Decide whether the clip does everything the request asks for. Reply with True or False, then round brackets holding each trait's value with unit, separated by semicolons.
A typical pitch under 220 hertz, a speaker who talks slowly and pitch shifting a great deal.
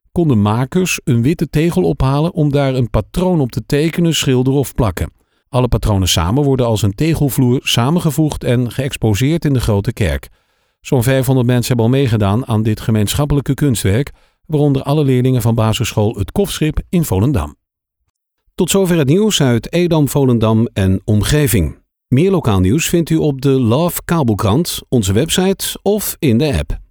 False (135 Hz; 165 wpm; 5.7 semitones)